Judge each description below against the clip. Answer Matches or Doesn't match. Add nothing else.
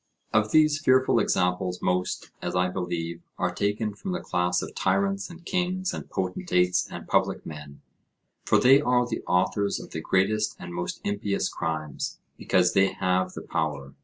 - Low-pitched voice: Matches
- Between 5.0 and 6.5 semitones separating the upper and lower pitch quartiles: Doesn't match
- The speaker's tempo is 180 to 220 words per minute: Doesn't match